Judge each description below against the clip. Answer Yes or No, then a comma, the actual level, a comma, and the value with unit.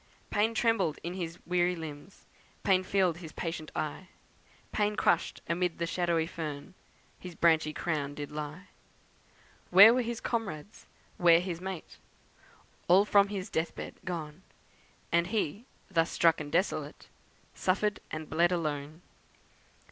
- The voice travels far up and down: No, average, 3.3 semitones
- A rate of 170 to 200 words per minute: No, slow, 135 wpm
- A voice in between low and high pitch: Yes, medium, 175 Hz